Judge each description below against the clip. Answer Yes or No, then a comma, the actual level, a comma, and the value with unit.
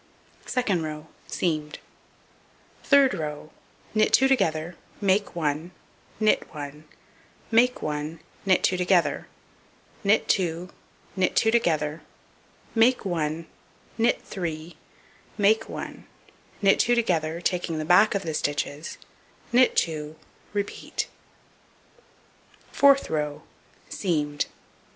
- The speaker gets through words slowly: Yes, slow, 105 wpm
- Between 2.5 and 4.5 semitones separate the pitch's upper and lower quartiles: No, average, 5.2 semitones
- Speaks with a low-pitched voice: No, medium, 175 Hz